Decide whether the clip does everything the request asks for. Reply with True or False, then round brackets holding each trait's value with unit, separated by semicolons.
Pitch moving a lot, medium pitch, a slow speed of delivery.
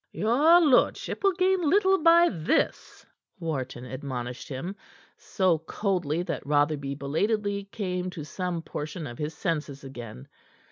True (7.1 semitones; 170 Hz; 130 wpm)